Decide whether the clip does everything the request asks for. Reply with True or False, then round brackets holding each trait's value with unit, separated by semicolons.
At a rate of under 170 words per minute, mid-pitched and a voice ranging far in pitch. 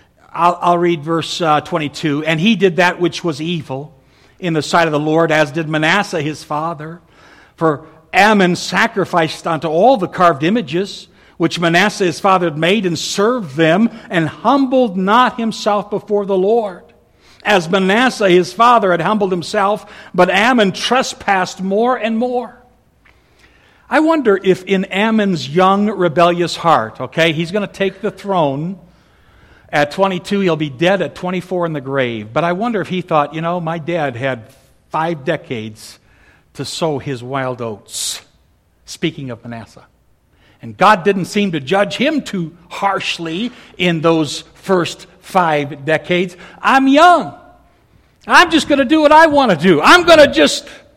False (160 wpm; 175 Hz; 4.5 semitones)